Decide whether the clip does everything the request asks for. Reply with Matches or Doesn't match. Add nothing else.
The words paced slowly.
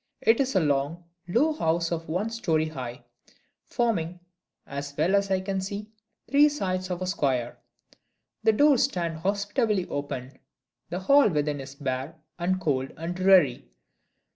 Doesn't match